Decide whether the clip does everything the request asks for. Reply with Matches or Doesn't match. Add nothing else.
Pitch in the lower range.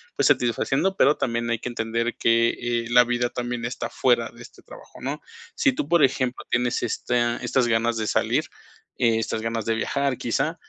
Matches